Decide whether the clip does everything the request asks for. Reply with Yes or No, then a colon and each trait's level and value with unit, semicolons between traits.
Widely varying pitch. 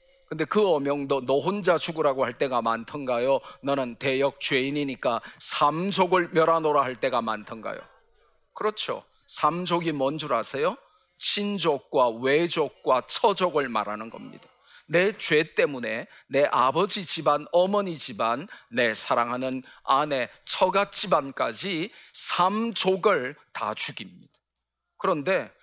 Yes: wide, 5.7 semitones